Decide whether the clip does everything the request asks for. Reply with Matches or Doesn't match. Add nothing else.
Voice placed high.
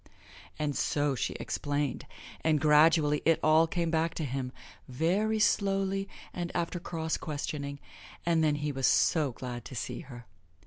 Doesn't match